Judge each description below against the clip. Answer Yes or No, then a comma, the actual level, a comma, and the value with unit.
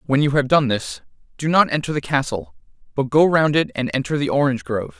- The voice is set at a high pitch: No, medium, 140 Hz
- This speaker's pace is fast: Yes, fast, 230 wpm